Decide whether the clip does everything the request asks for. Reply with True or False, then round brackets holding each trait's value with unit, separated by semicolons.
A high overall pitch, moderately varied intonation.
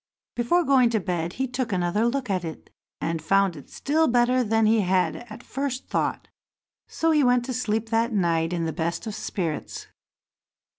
False (225 Hz; 5.9 semitones)